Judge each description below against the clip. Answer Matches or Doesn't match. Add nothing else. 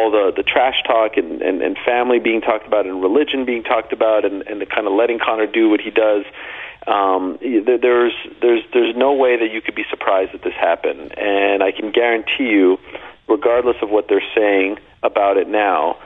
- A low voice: Matches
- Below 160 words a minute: Doesn't match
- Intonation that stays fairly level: Doesn't match